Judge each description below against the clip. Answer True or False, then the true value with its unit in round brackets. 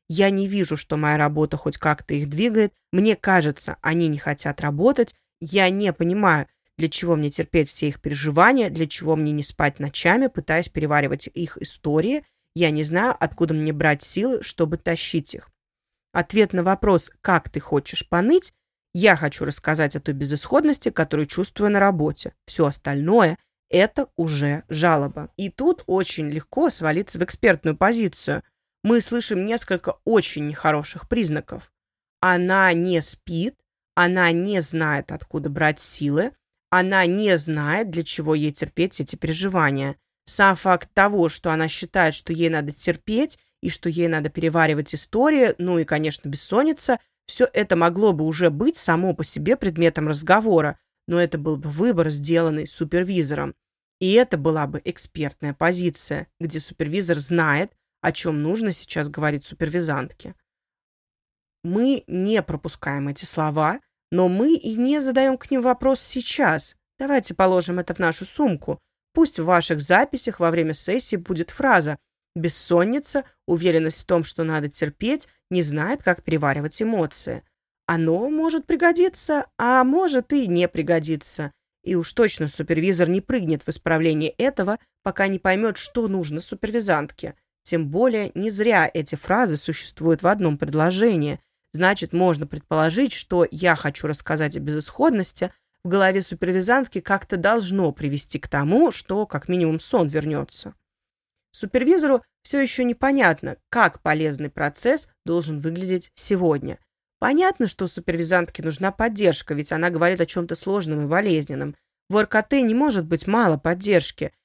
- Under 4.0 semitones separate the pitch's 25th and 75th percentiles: False (4.7 semitones)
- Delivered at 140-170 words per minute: True (145 wpm)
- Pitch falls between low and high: True (175 Hz)